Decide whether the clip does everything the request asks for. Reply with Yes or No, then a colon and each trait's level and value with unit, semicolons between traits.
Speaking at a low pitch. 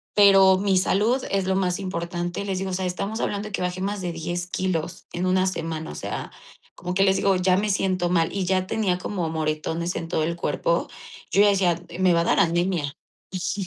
No: medium, 185 Hz